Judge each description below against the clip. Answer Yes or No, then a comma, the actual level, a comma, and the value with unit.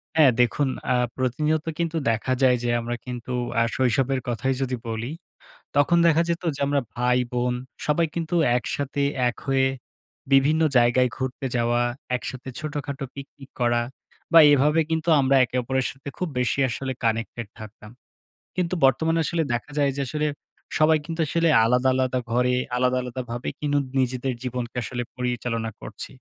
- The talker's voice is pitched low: Yes, low, 130 Hz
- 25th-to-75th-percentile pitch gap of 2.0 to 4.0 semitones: Yes, average, 2.9 semitones